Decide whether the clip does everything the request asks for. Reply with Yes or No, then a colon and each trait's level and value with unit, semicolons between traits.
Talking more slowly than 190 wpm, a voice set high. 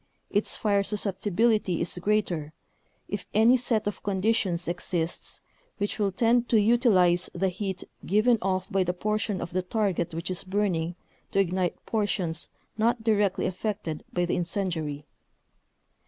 Yes: average, 140 wpm; high, 195 Hz